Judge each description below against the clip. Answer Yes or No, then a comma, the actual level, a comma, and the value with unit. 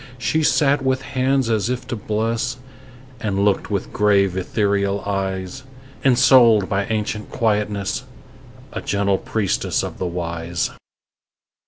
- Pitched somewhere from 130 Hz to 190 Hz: No, low, 105 Hz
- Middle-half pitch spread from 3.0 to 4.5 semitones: Yes, average, 3.6 semitones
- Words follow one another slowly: Yes, slow, 125 wpm